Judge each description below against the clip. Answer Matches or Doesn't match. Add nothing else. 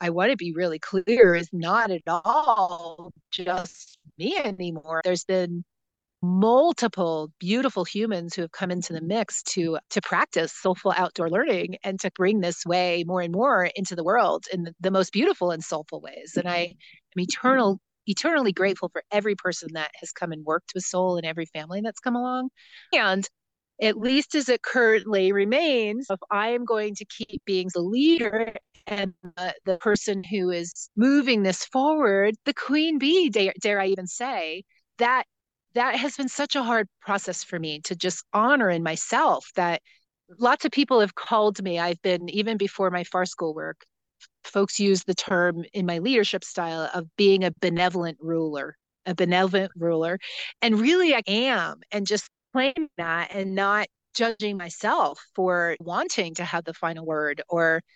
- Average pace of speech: Matches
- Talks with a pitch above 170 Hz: Matches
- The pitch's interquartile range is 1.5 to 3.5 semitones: Doesn't match